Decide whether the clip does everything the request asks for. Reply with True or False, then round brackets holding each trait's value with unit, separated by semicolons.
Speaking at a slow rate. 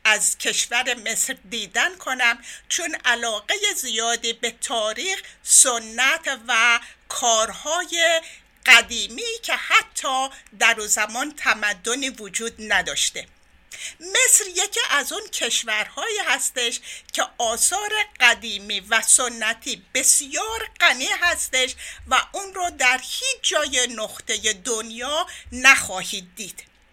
True (100 wpm)